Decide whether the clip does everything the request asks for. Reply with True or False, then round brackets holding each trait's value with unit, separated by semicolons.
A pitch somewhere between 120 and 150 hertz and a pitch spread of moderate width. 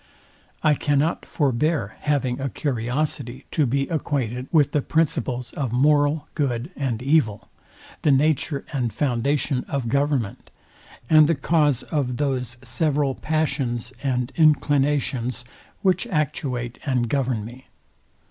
True (140 Hz; 3.1 semitones)